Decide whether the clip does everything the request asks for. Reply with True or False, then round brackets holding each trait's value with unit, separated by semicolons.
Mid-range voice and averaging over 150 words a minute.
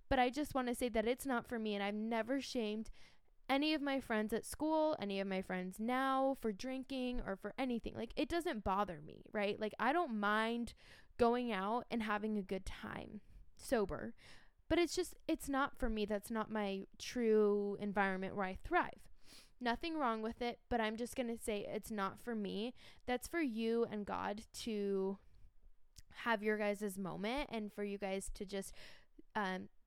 False (220 Hz; 190 wpm)